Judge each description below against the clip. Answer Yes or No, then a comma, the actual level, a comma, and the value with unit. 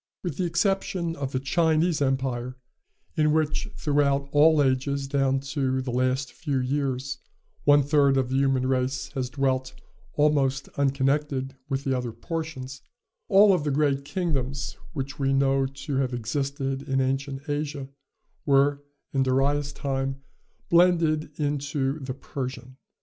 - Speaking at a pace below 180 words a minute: Yes, average, 140 wpm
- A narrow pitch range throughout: Yes, narrow, 1.8 semitones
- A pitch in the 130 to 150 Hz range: Yes, medium, 140 Hz